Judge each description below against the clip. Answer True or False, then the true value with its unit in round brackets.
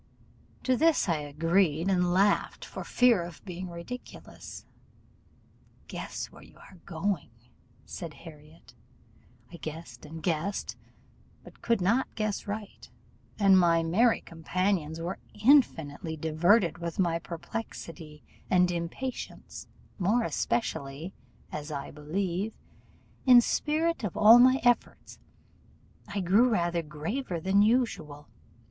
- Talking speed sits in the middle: False (115 wpm)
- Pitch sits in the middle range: True (180 Hz)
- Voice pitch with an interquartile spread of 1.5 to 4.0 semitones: False (4.7 semitones)